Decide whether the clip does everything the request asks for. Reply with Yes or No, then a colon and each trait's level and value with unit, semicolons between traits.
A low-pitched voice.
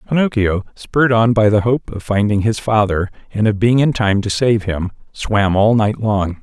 Yes: low, 110 Hz